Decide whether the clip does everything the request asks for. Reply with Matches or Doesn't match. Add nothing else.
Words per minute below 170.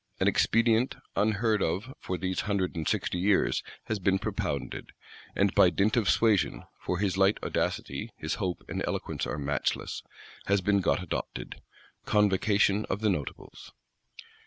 Matches